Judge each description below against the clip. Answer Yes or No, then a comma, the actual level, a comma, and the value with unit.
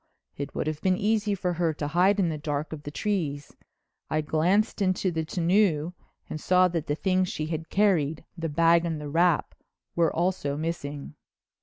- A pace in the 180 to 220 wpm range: Yes, average, 185 wpm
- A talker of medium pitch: Yes, medium, 165 Hz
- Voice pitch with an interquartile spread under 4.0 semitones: Yes, average, 3.2 semitones